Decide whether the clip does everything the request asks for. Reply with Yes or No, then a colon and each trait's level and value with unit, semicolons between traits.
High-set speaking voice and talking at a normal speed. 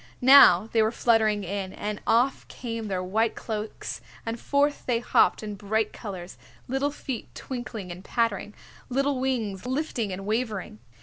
Yes: high, 220 Hz; average, 150 wpm